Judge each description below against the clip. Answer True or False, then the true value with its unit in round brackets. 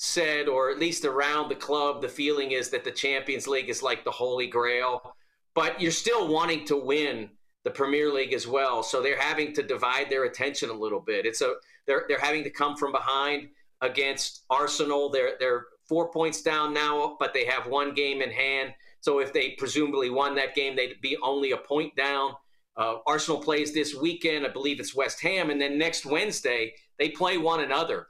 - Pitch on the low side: False (150 Hz)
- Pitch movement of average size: True (3.2 semitones)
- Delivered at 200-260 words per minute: True (205 wpm)